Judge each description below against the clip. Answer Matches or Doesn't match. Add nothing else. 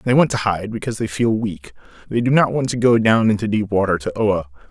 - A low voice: Matches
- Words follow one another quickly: Matches